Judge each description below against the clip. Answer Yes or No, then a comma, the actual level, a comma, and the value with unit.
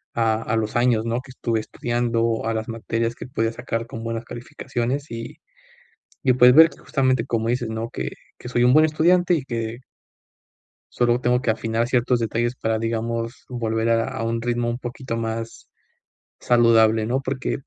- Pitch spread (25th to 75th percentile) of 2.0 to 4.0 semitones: No, narrow, 1.5 semitones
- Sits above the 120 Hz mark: No, low, 115 Hz